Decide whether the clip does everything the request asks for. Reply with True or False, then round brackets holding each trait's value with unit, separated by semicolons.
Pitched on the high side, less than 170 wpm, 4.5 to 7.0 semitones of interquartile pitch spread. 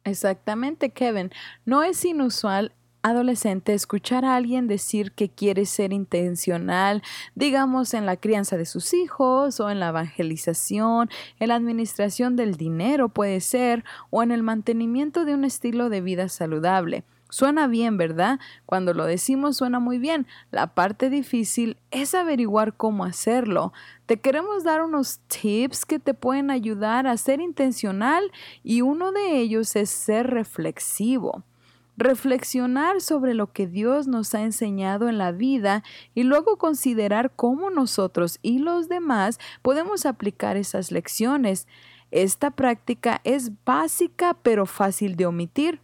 True (235 Hz; 140 wpm; 5.0 semitones)